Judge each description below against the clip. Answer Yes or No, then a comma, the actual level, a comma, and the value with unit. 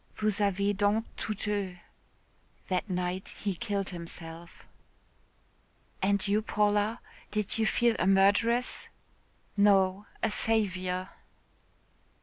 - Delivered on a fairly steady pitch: Yes, narrow, 2.2 semitones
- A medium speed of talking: No, slow, 105 wpm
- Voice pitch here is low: No, high, 200 Hz